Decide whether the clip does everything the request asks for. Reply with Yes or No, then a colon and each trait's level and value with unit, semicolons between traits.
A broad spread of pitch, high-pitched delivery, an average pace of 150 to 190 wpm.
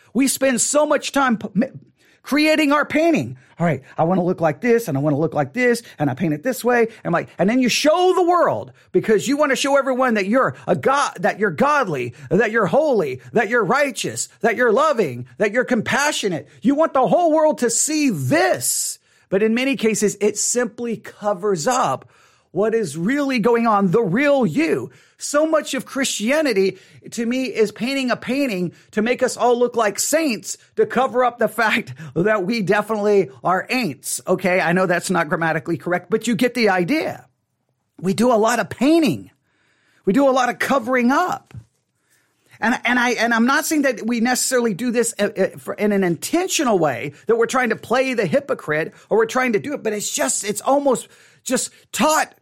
No: wide, 5.7 semitones; high, 230 Hz; average, 200 wpm